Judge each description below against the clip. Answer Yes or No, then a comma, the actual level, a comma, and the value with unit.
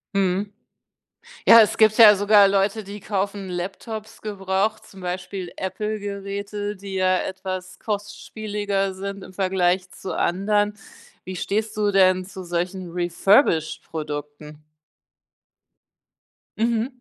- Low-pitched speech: No, high, 195 Hz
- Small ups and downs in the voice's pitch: Yes, narrow, 1.9 semitones